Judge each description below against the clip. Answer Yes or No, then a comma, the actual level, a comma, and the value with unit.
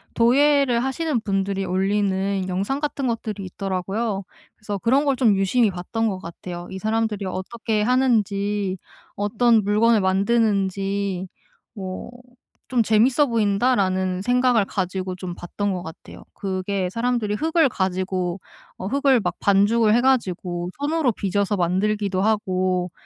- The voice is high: Yes, high, 205 Hz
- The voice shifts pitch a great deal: No, average, 3.8 semitones